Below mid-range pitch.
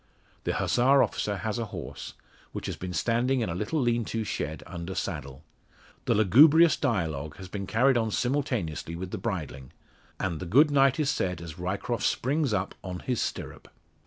Yes: low, 105 Hz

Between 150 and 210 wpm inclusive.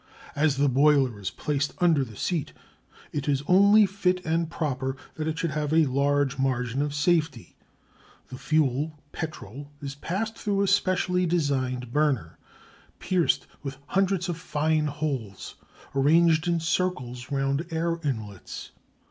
No: average, 140 wpm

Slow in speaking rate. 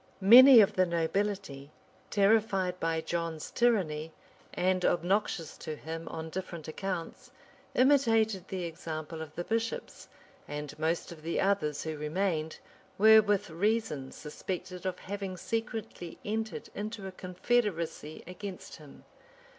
Yes: slow, 130 wpm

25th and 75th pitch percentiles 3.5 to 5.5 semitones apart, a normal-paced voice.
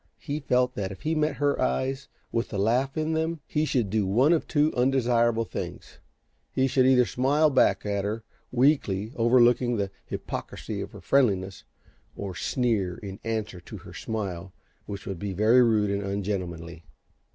Yes: average, 5.1 semitones; average, 170 wpm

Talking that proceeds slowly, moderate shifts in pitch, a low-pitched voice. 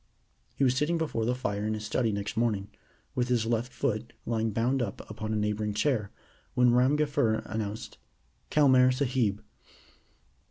No: average, 160 wpm; average, 3.1 semitones; low, 115 Hz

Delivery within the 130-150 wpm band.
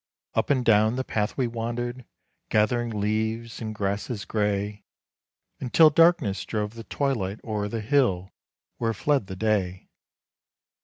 Yes: slow, 135 wpm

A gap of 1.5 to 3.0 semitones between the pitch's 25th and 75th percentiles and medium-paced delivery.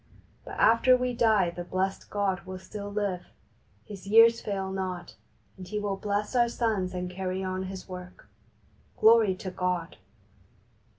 Yes: narrow, 2.4 semitones; average, 155 wpm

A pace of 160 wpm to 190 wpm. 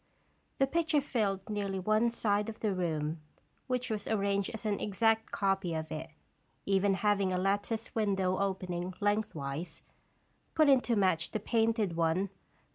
No: average, 150 wpm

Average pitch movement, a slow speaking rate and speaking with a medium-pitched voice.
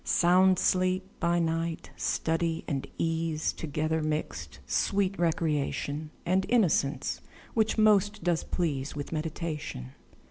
Yes: average, 3.1 semitones; slow, 110 wpm; medium, 165 Hz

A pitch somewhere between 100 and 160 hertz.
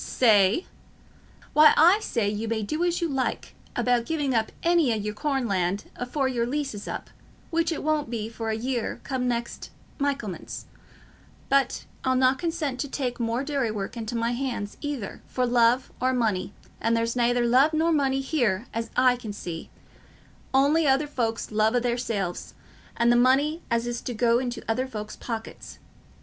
No: high, 245 Hz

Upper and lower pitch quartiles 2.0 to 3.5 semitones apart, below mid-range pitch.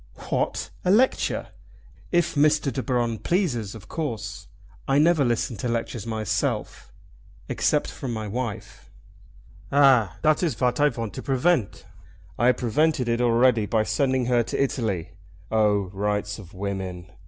No: average, 4.6 semitones; low, 120 Hz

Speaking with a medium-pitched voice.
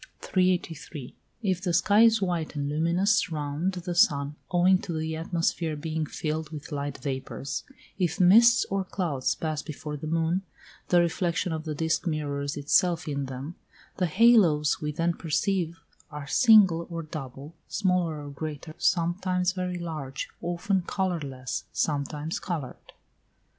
Yes: medium, 165 Hz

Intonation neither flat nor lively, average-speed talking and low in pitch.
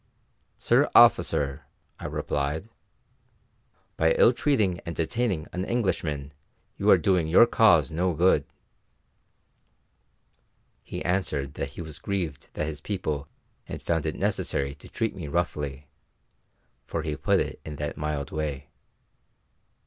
No: average, 4.2 semitones; slow, 130 wpm; very low, 80 Hz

